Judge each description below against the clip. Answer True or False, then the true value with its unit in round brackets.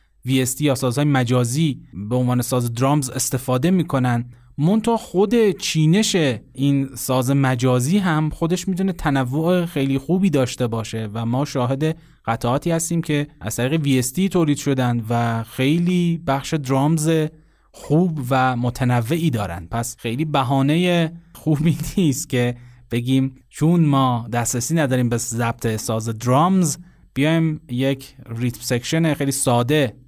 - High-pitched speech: False (135 Hz)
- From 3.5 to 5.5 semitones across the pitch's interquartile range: True (4.5 semitones)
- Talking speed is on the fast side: False (130 wpm)